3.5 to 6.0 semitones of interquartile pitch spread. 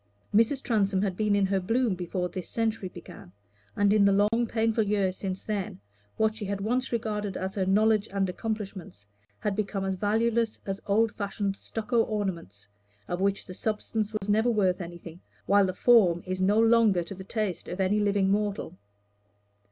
No: narrow, 2.5 semitones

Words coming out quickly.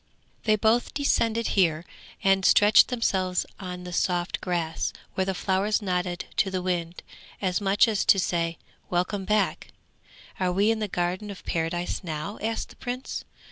No: average, 160 wpm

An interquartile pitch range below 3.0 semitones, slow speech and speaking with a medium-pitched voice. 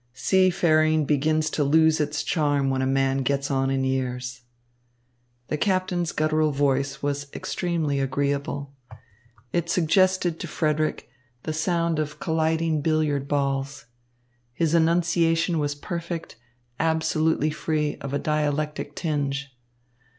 Yes: narrow, 2.5 semitones; slow, 120 wpm; medium, 155 Hz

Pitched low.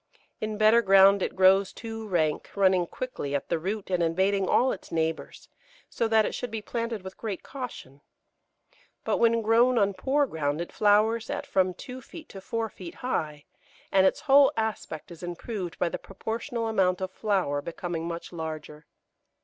No: high, 195 Hz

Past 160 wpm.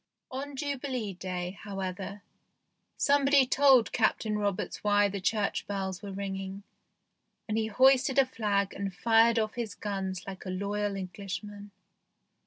No: slow, 135 wpm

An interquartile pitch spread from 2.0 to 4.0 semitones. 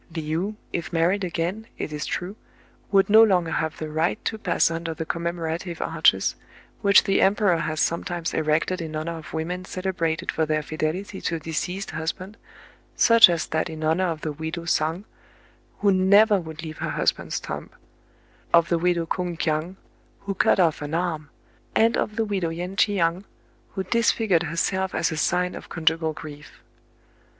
Yes: average, 3.0 semitones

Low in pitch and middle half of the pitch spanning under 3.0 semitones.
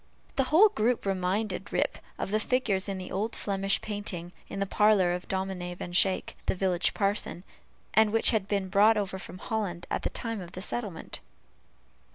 No: high, 195 Hz; narrow, 2.6 semitones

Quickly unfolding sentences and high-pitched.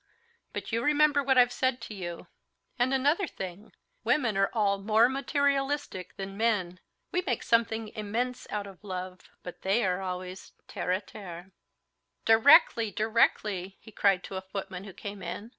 No: average, 160 wpm; high, 210 Hz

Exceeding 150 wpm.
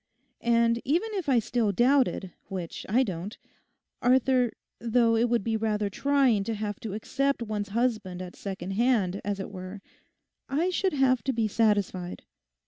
Yes: average, 160 wpm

